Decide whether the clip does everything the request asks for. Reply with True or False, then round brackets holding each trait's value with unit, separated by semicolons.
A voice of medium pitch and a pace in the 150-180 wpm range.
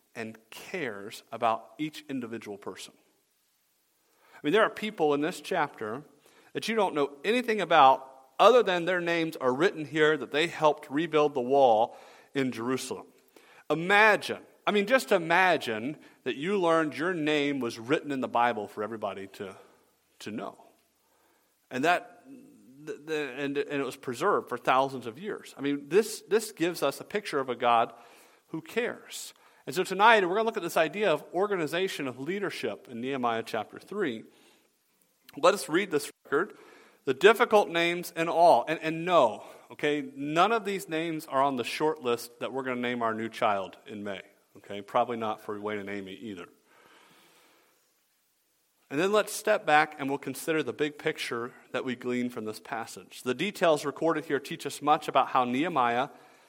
True (150 Hz; 175 wpm)